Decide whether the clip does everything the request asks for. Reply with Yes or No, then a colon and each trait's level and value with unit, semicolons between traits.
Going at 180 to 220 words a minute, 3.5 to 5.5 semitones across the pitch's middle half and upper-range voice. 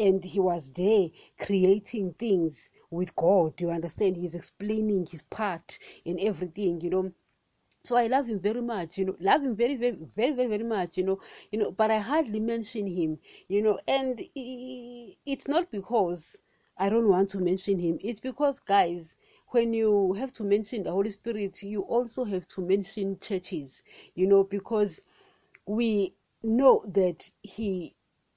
No: average, 165 wpm; average, 3.8 semitones; high, 205 Hz